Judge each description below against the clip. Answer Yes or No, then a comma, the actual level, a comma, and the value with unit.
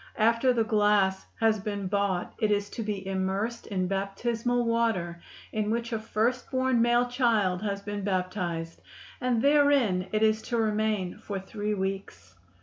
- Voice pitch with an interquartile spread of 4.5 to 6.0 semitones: No, average, 3.1 semitones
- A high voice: Yes, high, 210 Hz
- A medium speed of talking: Yes, average, 155 wpm